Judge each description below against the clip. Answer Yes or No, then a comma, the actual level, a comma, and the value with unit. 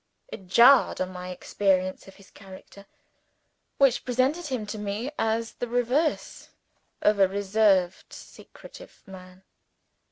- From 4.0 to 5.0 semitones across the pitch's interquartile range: Yes, average, 4.4 semitones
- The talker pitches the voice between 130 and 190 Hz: No, high, 205 Hz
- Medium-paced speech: No, slow, 125 wpm